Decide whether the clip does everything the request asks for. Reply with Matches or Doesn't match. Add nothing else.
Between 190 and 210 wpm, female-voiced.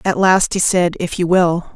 Doesn't match